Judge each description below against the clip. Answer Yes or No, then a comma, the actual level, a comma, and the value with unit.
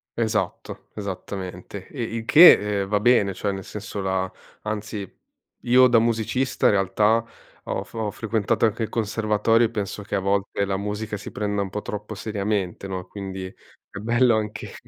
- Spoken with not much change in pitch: Yes, narrow, 2.2 semitones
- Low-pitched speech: Yes, low, 105 Hz